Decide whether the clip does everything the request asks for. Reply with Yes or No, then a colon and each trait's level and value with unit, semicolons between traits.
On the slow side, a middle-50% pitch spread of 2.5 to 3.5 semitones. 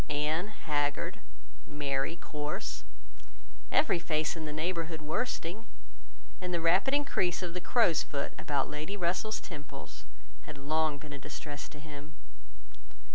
Yes: slow, 130 wpm; average, 3.1 semitones